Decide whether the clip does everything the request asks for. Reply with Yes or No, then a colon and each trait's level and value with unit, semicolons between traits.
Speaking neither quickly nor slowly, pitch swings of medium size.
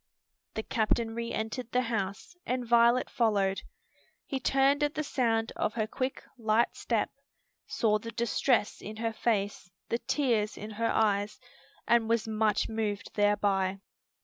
No: average, 145 wpm; narrow, 2.1 semitones